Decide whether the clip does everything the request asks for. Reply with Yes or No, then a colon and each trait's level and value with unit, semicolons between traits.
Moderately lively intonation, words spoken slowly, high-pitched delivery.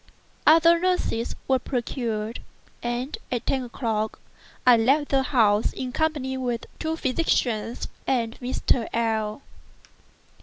Yes: average, 3.2 semitones; slow, 120 wpm; very high, 250 Hz